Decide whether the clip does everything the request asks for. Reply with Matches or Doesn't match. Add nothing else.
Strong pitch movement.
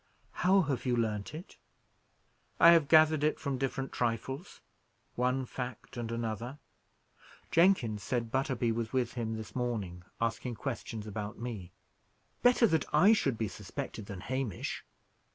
Doesn't match